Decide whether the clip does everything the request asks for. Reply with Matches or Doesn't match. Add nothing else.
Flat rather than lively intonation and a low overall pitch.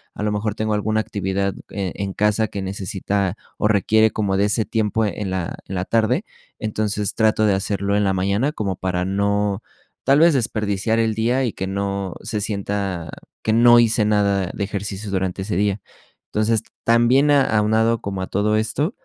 Matches